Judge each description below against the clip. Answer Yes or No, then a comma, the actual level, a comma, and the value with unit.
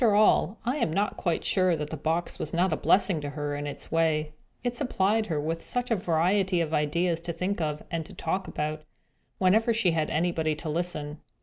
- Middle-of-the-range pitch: Yes, medium, 170 Hz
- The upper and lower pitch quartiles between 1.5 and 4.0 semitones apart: Yes, average, 3.7 semitones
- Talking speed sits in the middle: No, fast, 215 wpm